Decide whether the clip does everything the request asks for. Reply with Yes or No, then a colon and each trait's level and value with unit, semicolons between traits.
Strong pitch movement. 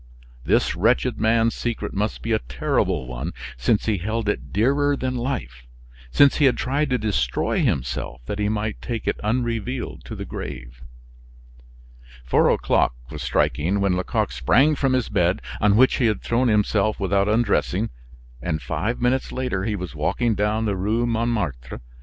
No: average, 4.8 semitones